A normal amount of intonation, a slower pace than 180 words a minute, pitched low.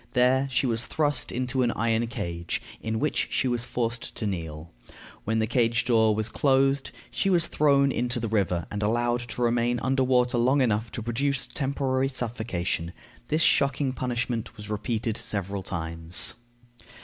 Yes: average, 3.2 semitones; average, 160 wpm; low, 120 Hz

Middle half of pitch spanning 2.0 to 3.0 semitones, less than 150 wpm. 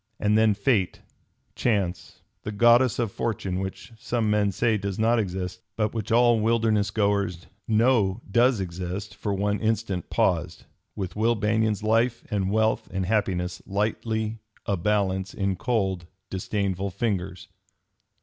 Yes: average, 2.7 semitones; average, 140 wpm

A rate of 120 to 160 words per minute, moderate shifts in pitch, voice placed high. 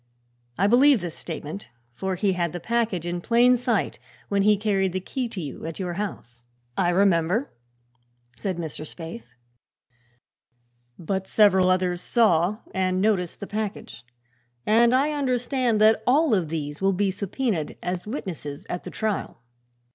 Yes: average, 150 wpm; average, 4.1 semitones; high, 195 Hz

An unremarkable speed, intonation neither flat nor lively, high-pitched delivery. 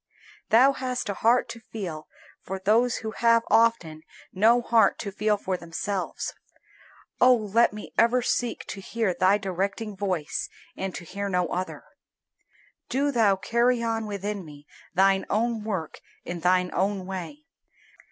Yes: average, 150 wpm; average, 3.6 semitones; high, 205 Hz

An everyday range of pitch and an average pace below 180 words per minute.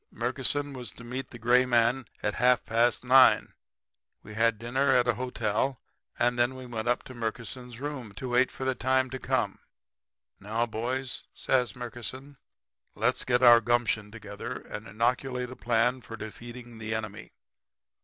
No: narrow, 2.0 semitones; average, 160 wpm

